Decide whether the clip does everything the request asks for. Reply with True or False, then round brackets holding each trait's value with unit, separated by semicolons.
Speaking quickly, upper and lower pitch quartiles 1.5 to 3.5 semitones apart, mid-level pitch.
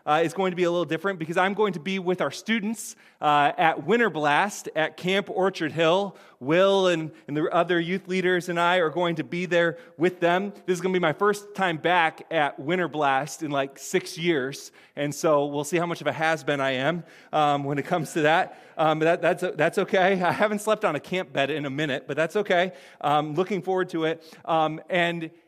True (230 wpm; 2.8 semitones; 170 Hz)